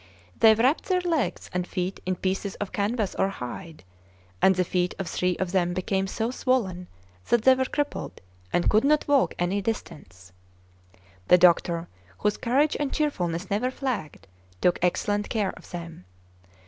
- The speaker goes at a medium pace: Yes, average, 160 wpm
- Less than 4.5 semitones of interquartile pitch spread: No, wide, 5.5 semitones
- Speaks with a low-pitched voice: No, high, 195 Hz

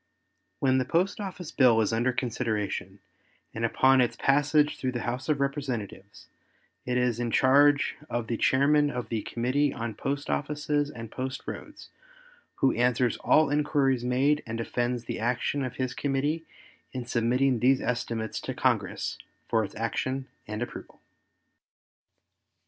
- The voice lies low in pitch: Yes, low, 130 Hz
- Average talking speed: Yes, average, 150 wpm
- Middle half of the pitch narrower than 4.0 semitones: Yes, average, 3.2 semitones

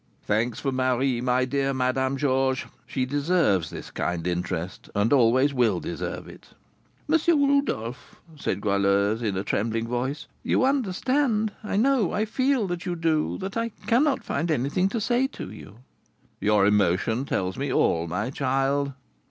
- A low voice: Yes, low, 130 Hz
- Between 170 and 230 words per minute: No, average, 155 wpm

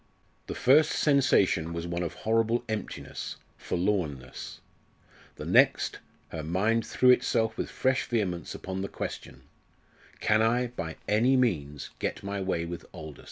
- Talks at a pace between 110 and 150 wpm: Yes, average, 140 wpm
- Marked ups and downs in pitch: Yes, wide, 5.7 semitones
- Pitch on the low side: Yes, low, 100 Hz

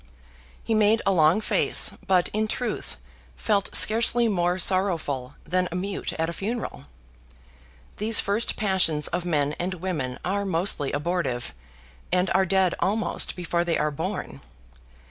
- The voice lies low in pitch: No, medium, 185 Hz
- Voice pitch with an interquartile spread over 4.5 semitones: No, average, 3.8 semitones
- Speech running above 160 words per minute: No, average, 145 wpm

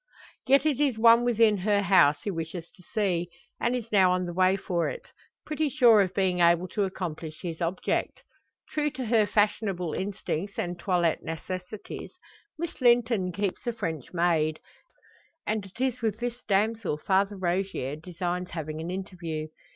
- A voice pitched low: No, high, 190 Hz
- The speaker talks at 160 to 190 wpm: Yes, average, 165 wpm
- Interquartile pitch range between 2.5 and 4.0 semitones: No, average, 4.4 semitones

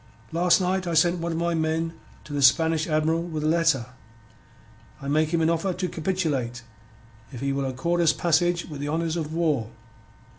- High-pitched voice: No, medium, 160 Hz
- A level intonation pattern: Yes, narrow, 2.2 semitones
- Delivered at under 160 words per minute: No, average, 185 wpm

